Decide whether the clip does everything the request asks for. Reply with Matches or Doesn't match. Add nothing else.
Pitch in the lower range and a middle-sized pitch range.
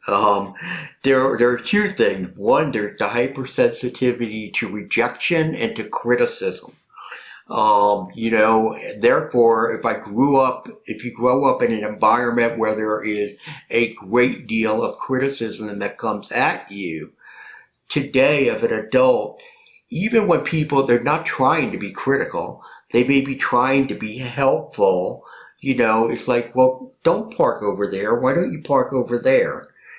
Matches